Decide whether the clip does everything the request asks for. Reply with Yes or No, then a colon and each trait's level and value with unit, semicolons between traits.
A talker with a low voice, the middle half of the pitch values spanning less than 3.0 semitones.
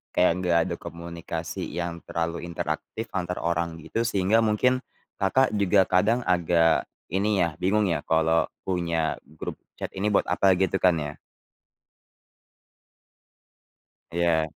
Yes: very low, 85 Hz; narrow, 2.6 semitones